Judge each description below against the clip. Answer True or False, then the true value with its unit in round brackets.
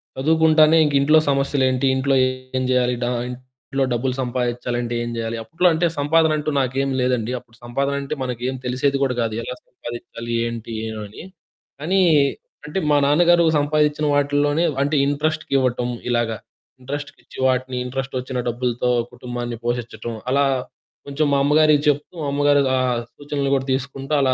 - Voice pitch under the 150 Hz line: True (135 Hz)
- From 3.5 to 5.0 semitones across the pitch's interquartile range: False (2.8 semitones)